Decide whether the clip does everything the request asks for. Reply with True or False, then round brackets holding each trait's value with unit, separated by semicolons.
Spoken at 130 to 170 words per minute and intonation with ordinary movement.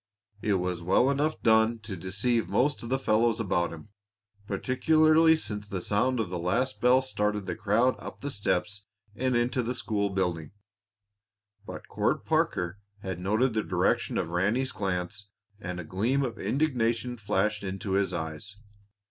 True (160 wpm; 4.8 semitones)